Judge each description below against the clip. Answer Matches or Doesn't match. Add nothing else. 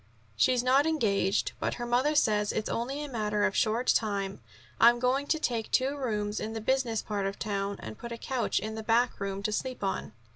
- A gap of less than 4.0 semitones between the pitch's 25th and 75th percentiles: Matches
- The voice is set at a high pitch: Matches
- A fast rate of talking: Matches